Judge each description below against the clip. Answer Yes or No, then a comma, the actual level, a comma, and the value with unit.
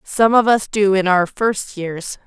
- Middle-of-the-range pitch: No, high, 200 Hz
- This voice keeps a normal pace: No, fast, 210 wpm